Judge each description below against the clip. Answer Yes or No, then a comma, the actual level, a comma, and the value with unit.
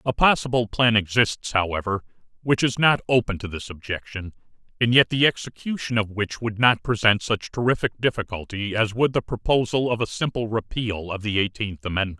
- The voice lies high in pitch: No, low, 110 Hz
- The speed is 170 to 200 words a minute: Yes, average, 175 wpm